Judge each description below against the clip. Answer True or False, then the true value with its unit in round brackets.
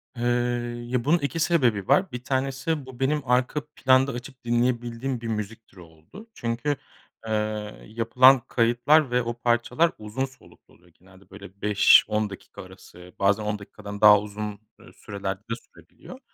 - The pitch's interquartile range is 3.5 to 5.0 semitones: True (3.9 semitones)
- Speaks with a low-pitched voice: True (120 Hz)